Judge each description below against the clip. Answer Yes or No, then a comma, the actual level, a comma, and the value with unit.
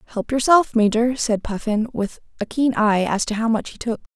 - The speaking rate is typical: No, fast, 215 wpm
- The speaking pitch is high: Yes, high, 225 Hz